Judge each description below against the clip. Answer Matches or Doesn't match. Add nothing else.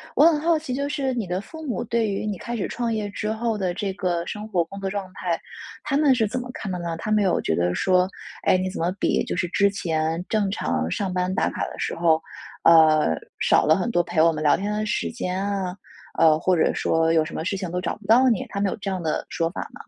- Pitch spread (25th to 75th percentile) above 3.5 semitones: Matches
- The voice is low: Doesn't match